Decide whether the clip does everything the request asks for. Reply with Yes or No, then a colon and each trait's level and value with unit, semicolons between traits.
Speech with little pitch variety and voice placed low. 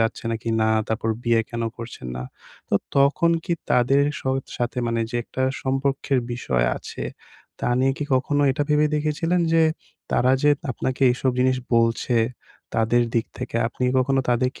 No: average, 3.0 semitones; low, 130 Hz